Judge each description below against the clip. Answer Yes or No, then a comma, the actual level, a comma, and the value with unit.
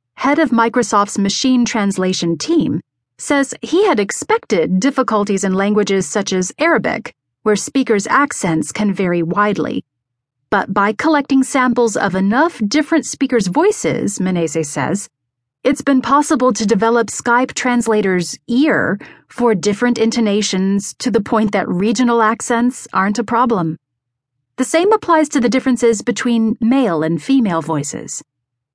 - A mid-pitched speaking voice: No, high, 220 Hz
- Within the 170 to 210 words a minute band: No, slow, 135 wpm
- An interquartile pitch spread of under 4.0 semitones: No, wide, 5.5 semitones